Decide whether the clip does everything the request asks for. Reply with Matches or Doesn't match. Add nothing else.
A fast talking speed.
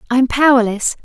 Doesn't match